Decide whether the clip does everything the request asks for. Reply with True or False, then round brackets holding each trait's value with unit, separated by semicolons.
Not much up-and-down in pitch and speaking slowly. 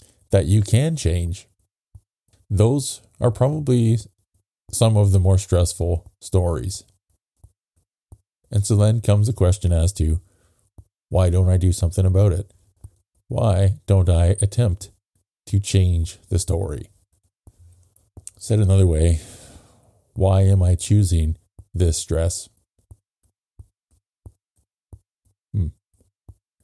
True (2.3 semitones; 105 wpm)